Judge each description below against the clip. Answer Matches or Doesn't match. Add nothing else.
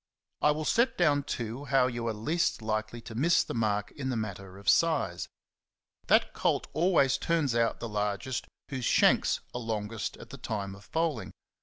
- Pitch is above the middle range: Doesn't match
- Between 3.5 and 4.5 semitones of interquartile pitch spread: Doesn't match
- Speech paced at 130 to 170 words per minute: Doesn't match